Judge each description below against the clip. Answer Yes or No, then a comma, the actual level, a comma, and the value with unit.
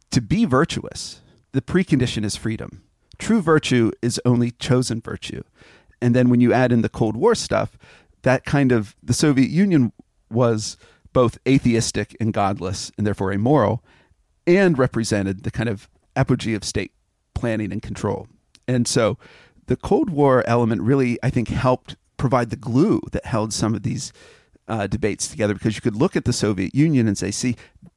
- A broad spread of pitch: No, average, 3.3 semitones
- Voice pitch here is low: Yes, low, 120 Hz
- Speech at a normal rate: Yes, average, 170 wpm